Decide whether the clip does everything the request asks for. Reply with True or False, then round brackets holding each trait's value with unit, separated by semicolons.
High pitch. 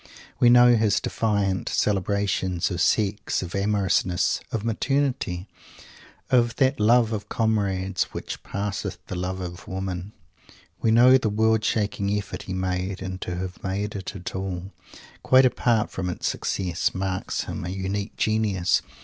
False (100 Hz)